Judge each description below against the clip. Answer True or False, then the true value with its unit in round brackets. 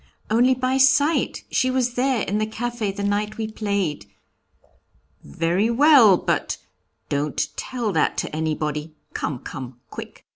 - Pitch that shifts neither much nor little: False (7.7 semitones)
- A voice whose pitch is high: True (215 Hz)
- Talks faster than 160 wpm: False (140 wpm)